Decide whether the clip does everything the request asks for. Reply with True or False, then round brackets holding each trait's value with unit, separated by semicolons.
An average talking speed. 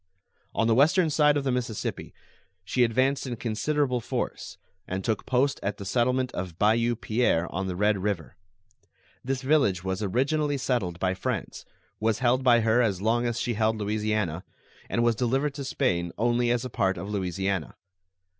True (175 wpm)